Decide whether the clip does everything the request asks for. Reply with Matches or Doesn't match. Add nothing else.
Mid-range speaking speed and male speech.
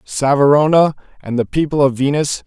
Matches